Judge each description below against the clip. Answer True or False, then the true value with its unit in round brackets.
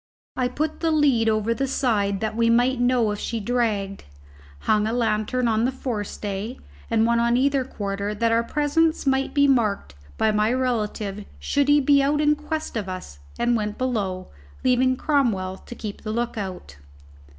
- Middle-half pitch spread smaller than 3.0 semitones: False (3.8 semitones)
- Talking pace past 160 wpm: True (180 wpm)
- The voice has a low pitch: False (235 Hz)